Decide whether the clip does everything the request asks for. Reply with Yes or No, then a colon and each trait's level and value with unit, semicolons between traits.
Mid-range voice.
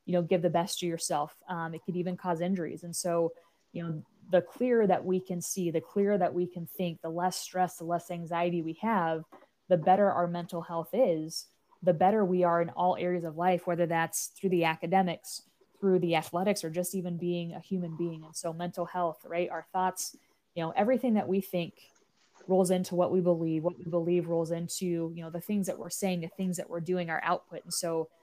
Yes: medium, 175 Hz